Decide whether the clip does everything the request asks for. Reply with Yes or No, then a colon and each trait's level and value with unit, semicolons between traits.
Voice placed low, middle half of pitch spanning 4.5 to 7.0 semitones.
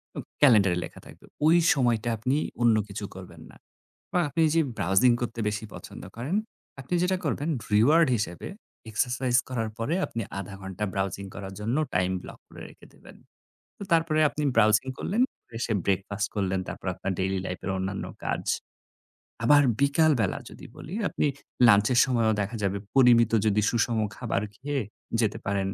Yes: low, 115 Hz; average, 5.1 semitones